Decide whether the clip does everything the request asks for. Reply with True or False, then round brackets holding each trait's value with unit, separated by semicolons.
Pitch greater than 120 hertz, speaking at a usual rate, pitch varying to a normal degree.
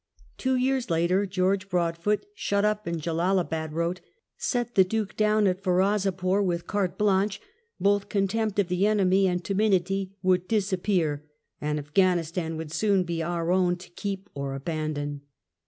True (185 Hz; 155 wpm; 3.0 semitones)